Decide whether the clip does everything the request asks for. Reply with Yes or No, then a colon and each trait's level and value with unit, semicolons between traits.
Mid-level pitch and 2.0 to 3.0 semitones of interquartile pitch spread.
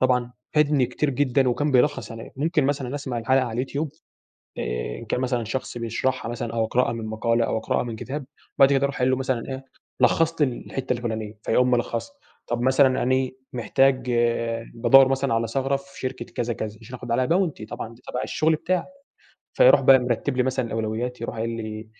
No: low, 125 Hz; average, 2.7 semitones